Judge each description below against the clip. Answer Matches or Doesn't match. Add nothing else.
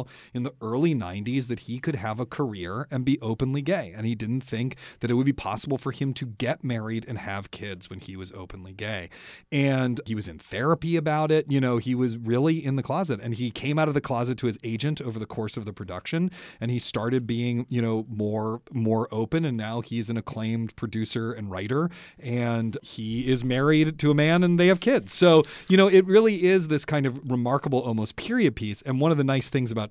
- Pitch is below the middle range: Matches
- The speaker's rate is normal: Doesn't match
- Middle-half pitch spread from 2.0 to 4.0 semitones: Doesn't match